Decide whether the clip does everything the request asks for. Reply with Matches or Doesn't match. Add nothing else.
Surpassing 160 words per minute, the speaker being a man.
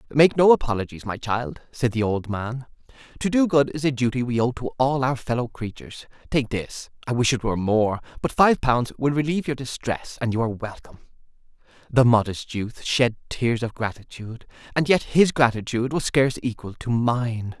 Matches